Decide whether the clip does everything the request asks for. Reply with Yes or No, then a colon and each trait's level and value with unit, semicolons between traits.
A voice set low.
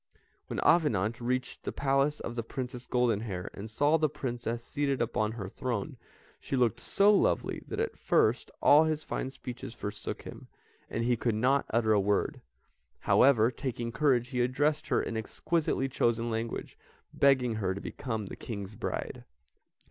Yes: low, 120 Hz